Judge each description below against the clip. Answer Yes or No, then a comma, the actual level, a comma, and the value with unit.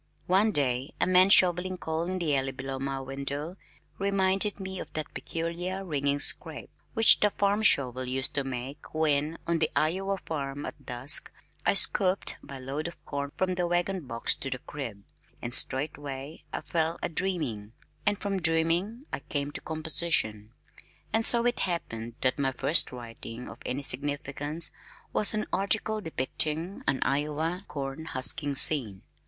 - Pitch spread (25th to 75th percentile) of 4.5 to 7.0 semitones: Yes, average, 5.1 semitones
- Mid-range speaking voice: Yes, medium, 155 Hz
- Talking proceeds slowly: No, average, 160 wpm